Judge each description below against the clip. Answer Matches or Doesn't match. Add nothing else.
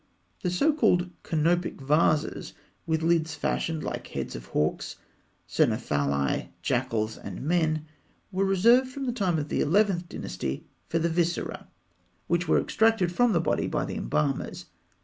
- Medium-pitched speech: Matches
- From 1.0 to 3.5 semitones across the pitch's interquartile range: Doesn't match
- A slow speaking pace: Doesn't match